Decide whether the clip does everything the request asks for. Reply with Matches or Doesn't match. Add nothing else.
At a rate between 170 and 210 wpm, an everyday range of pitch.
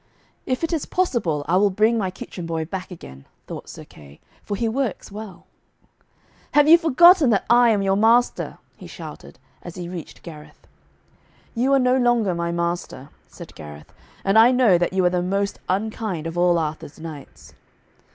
Doesn't match